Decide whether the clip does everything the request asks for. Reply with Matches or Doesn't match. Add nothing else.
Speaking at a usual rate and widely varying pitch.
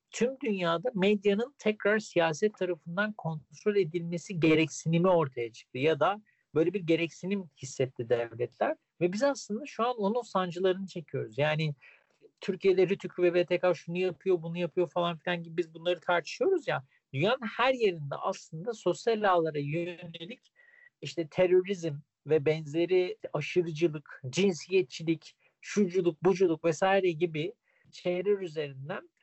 Doesn't match